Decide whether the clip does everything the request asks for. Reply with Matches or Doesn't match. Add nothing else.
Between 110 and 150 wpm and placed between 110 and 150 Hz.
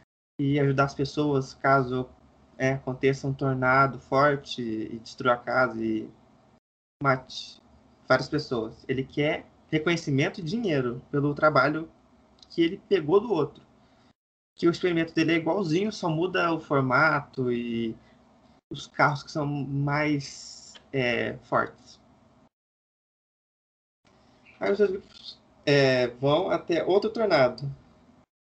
Matches